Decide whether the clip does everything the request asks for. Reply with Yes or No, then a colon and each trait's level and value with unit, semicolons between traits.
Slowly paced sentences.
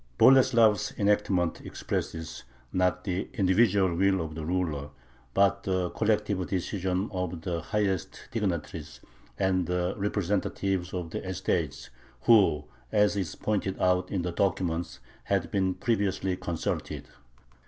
Yes: slow, 120 wpm